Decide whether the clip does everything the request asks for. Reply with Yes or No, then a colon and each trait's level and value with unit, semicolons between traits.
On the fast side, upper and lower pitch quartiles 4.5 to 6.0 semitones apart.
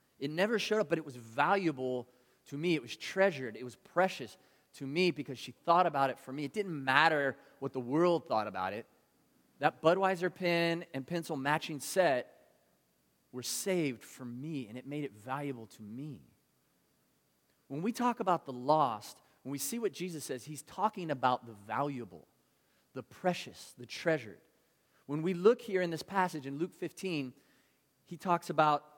No: average, 180 wpm; average, 5.3 semitones